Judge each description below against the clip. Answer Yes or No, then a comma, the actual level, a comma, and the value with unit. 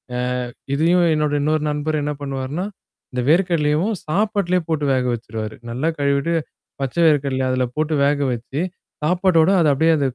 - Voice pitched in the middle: Yes, medium, 150 Hz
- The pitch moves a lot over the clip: No, average, 3.4 semitones